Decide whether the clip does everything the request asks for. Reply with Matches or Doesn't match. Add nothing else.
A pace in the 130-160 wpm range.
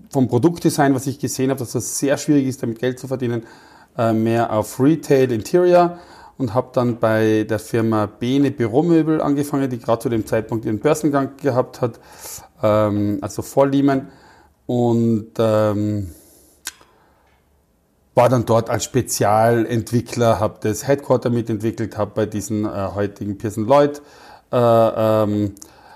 Matches